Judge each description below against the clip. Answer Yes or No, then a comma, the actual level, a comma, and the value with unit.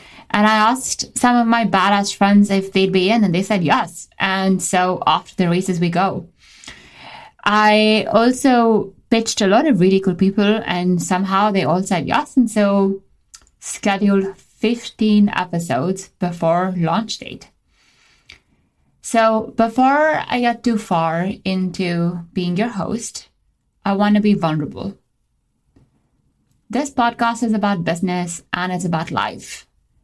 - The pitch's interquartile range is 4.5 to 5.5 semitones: No, average, 3.4 semitones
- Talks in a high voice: Yes, high, 200 Hz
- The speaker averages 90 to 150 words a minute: Yes, average, 140 wpm